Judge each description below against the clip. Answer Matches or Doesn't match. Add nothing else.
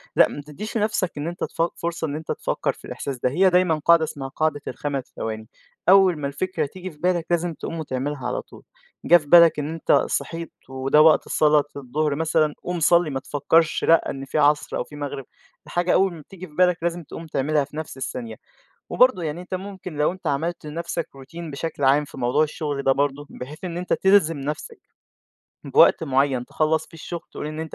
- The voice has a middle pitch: Matches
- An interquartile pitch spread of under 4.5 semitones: Matches